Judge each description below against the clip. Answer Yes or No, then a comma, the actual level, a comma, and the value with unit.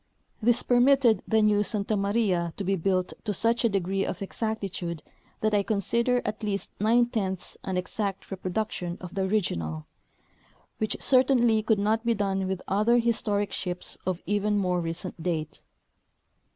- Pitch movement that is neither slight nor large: Yes, average, 3.0 semitones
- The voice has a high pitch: Yes, high, 200 Hz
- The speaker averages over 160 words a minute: No, average, 155 wpm